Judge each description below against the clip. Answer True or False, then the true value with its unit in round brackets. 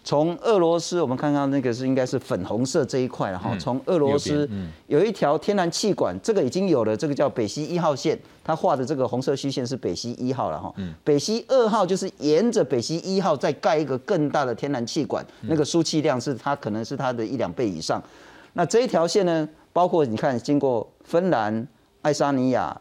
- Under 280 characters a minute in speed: False (320 characters per minute)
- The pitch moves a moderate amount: True (4.7 semitones)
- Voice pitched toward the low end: False (145 Hz)